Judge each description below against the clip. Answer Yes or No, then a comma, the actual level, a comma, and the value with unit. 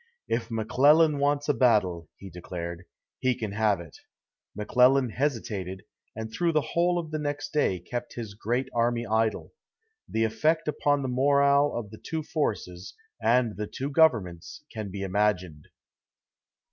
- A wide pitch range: Yes, wide, 5.9 semitones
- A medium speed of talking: Yes, average, 150 wpm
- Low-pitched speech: Yes, low, 115 Hz